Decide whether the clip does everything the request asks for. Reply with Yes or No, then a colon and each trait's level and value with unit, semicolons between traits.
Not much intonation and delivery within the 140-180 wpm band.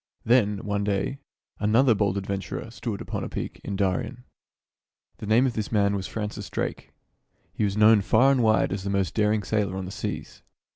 No: narrow, 2.0 semitones; average, 190 wpm